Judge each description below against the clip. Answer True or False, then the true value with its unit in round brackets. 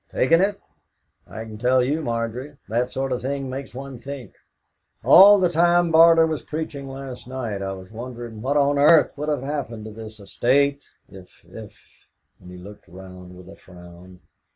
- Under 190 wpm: True (180 wpm)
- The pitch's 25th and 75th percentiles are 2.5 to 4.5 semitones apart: False (5.1 semitones)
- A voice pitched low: True (130 Hz)